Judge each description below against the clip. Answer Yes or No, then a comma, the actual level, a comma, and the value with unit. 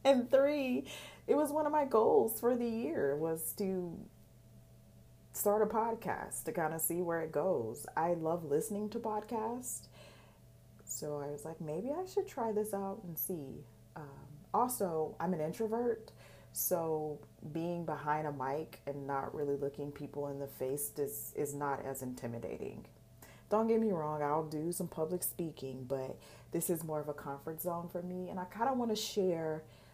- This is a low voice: No, medium, 165 Hz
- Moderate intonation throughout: No, wide, 6.6 semitones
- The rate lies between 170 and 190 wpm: Yes, average, 180 wpm